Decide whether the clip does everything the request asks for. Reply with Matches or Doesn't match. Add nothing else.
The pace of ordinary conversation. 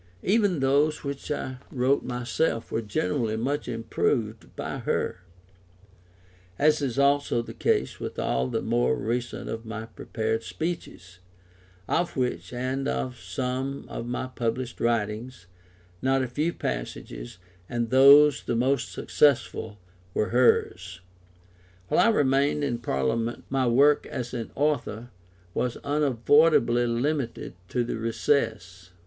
Doesn't match